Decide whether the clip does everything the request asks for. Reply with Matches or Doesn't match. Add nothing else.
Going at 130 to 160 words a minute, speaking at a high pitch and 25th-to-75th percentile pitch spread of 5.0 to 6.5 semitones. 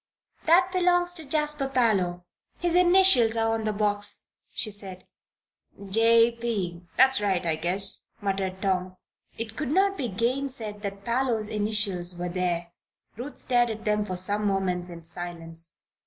Matches